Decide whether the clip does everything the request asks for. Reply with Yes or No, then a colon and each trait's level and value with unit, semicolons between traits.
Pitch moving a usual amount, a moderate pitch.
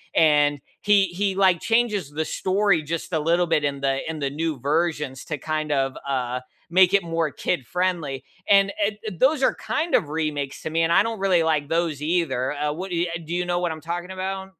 Yes: average, 4.1 semitones; medium, 165 Hz